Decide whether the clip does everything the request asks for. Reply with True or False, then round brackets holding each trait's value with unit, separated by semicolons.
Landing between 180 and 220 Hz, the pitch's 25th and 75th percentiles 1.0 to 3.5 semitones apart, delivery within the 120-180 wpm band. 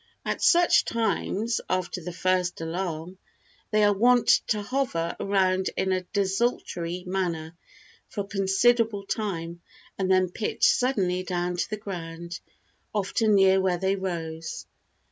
True (190 Hz; 3.0 semitones; 135 wpm)